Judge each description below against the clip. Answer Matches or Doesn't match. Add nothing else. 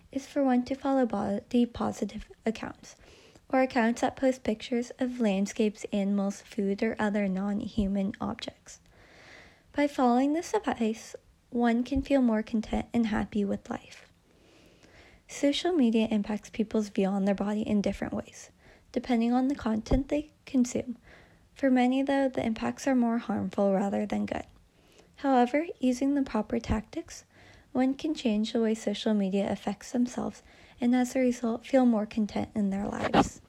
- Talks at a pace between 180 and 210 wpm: Doesn't match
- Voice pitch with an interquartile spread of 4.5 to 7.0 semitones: Doesn't match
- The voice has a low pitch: Doesn't match